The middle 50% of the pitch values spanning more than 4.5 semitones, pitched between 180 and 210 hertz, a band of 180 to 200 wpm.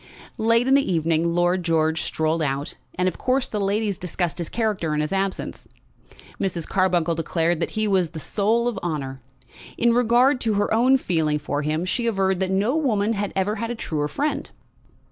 Yes: wide, 5.5 semitones; high, 190 Hz; average, 190 wpm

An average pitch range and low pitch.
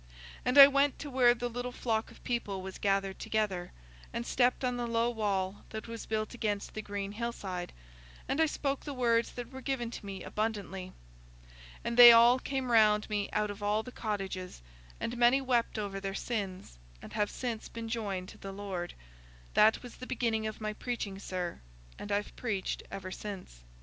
No: average, 3.5 semitones; high, 220 Hz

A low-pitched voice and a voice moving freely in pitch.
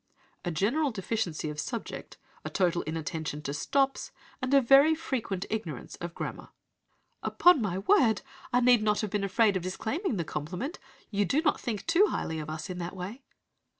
No: high, 210 Hz; wide, 7.0 semitones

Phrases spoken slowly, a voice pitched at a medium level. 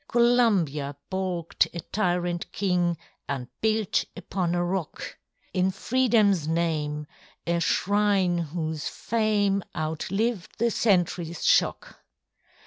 Yes: slow, 100 wpm; medium, 180 Hz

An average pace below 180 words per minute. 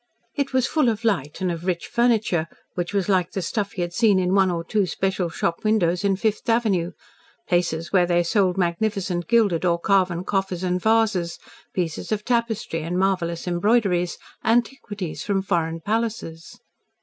Yes: average, 170 wpm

